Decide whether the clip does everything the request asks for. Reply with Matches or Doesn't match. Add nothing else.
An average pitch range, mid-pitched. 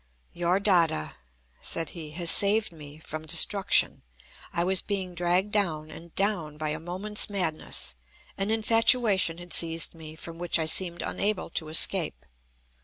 Matches